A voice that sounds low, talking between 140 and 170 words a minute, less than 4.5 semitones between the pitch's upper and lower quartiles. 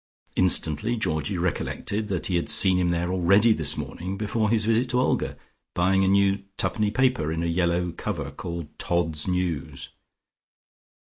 Yes: very low, 90 Hz; average, 160 wpm; average, 3.6 semitones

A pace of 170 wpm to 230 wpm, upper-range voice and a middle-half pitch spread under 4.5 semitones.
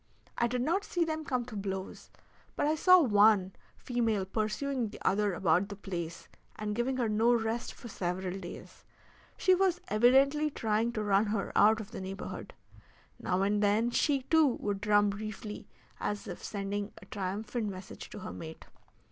Yes: average, 175 wpm; high, 215 Hz; average, 3.6 semitones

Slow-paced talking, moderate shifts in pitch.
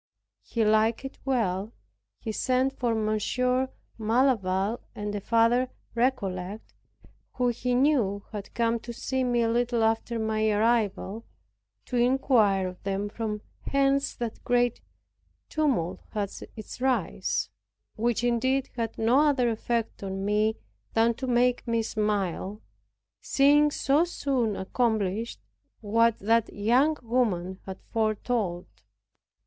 Yes: slow, 125 wpm; average, 3.0 semitones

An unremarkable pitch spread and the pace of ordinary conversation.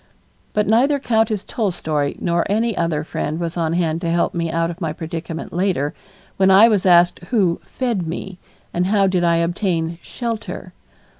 Yes: average, 3.8 semitones; average, 170 wpm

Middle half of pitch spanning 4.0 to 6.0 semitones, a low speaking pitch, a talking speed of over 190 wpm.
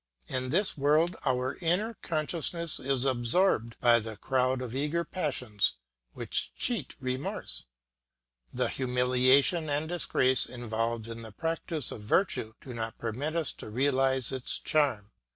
No: average, 4.6 semitones; low, 130 Hz; slow, 135 wpm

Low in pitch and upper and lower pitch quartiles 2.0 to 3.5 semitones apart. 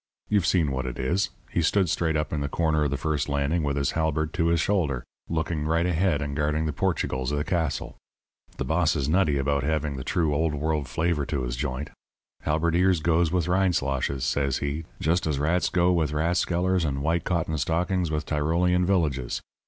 Yes: very low, 80 Hz; average, 3.1 semitones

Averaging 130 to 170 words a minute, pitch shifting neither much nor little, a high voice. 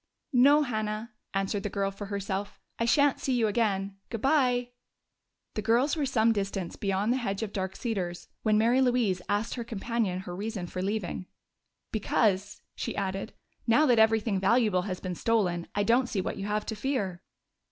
No: average, 180 wpm; average, 3.3 semitones; high, 215 Hz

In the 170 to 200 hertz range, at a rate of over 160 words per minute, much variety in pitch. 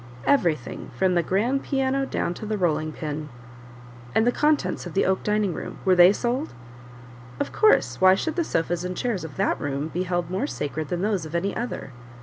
Yes: medium, 185 Hz; average, 200 wpm; wide, 6.3 semitones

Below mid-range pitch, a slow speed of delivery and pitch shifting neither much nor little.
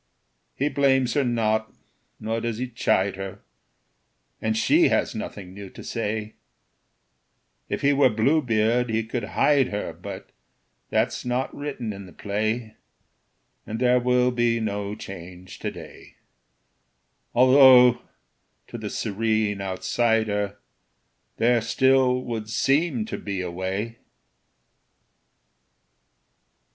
Yes: low, 115 Hz; slow, 115 wpm; average, 3.4 semitones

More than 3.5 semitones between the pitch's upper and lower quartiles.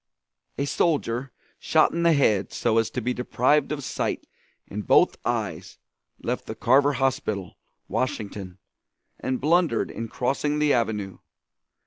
Yes: average, 4.7 semitones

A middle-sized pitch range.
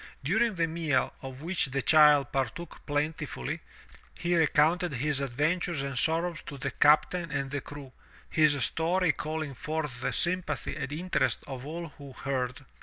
Yes: average, 3.2 semitones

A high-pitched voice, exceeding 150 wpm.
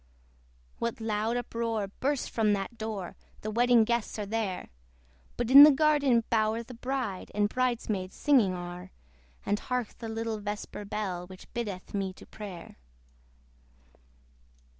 No: high, 220 Hz; average, 140 wpm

